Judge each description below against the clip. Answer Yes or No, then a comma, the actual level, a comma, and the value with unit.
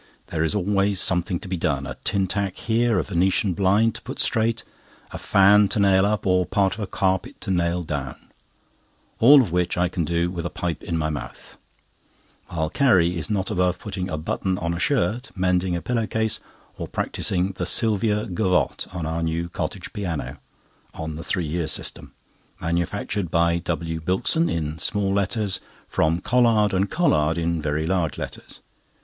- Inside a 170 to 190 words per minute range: Yes, average, 180 wpm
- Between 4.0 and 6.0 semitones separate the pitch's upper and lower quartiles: No, average, 3.3 semitones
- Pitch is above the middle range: No, very low, 90 Hz